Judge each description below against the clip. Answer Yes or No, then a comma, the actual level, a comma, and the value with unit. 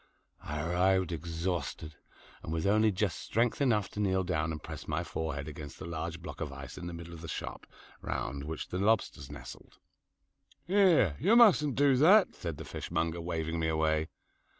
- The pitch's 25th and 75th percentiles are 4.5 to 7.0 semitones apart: Yes, average, 4.9 semitones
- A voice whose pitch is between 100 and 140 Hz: No, very low, 85 Hz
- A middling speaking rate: Yes, average, 180 wpm